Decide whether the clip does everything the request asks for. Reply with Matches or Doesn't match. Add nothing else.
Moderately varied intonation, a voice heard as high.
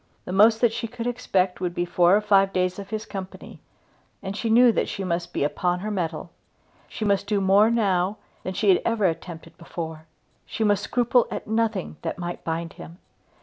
Matches